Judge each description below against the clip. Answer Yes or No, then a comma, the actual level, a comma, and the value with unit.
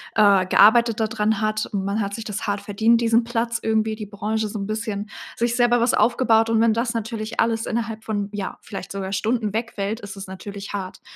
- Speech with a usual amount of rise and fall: No, narrow, 2.1 semitones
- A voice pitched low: No, high, 220 Hz